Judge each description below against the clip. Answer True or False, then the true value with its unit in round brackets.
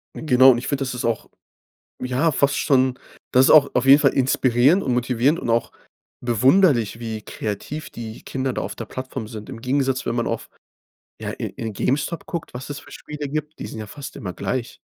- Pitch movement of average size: True (3.2 semitones)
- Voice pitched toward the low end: True (130 Hz)